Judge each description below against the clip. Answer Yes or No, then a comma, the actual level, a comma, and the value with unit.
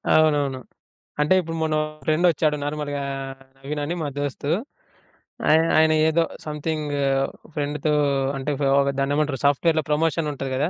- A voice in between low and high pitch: Yes, medium, 150 Hz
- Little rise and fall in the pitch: Yes, narrow, 1.6 semitones